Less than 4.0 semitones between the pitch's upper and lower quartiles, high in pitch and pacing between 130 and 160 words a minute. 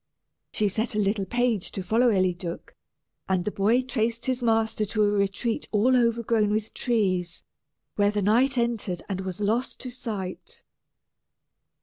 Yes: average, 3.1 semitones; high, 215 Hz; average, 150 wpm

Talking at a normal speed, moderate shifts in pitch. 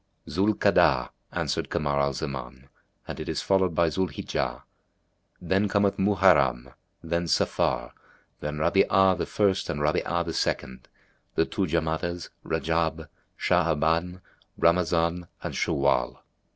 No: slow, 125 wpm; average, 4.1 semitones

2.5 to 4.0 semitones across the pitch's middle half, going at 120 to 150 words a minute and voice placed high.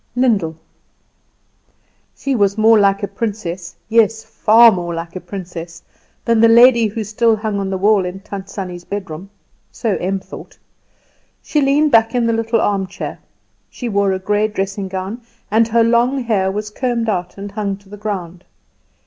No: average, 3.0 semitones; average, 170 wpm; high, 205 Hz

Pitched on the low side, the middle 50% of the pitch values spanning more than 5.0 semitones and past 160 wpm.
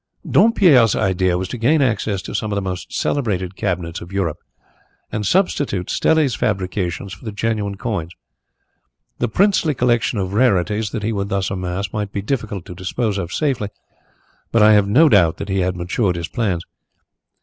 No: low, 100 Hz; average, 3.8 semitones; average, 175 wpm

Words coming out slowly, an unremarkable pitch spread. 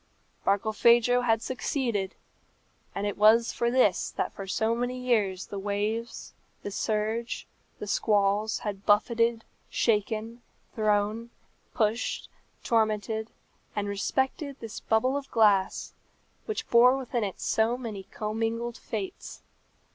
No: slow, 115 wpm; narrow, 2.3 semitones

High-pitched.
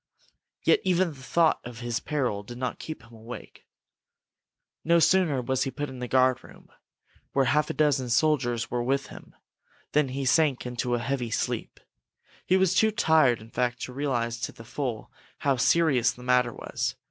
No: low, 130 Hz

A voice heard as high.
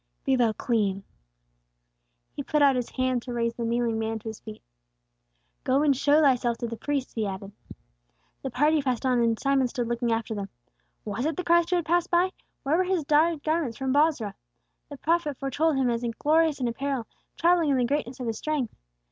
Yes: very high, 260 Hz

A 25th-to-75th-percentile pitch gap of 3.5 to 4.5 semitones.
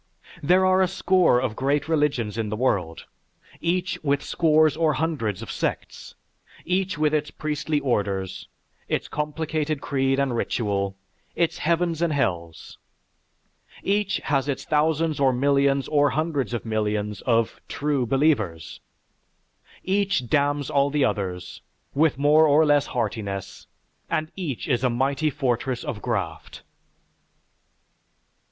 No: average, 5.0 semitones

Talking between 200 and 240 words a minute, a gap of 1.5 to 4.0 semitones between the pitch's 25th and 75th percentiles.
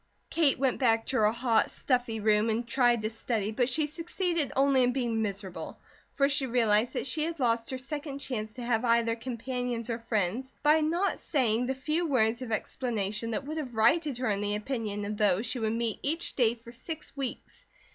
Yes: fast, 205 wpm; average, 3.6 semitones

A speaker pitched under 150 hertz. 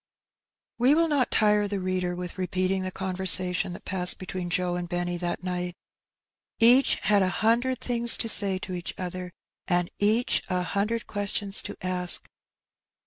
No: medium, 185 Hz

